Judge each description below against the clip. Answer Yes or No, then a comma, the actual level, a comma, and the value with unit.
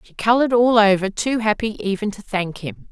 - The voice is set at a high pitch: Yes, high, 210 Hz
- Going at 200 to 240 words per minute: Yes, fast, 205 wpm